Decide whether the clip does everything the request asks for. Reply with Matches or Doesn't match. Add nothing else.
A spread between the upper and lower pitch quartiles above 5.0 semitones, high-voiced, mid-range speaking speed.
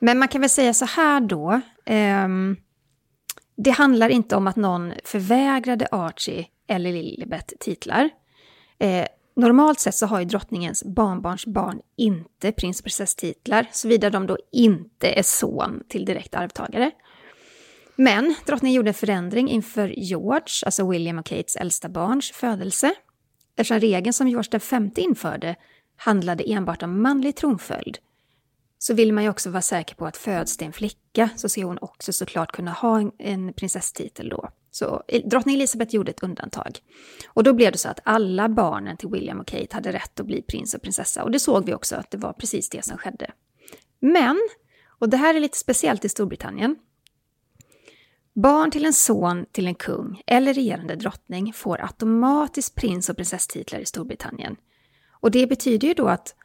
Matches